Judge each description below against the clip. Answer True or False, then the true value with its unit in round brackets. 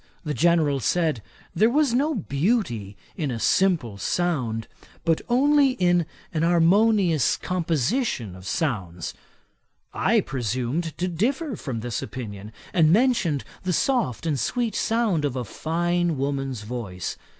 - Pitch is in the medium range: True (160 Hz)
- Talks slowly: True (130 wpm)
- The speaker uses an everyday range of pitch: False (7.8 semitones)